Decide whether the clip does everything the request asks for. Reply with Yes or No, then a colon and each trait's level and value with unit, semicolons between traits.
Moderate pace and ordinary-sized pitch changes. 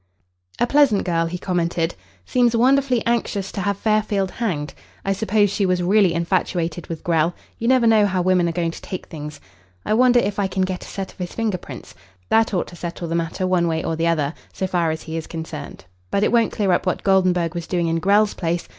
No: fast, 225 wpm; average, 3.7 semitones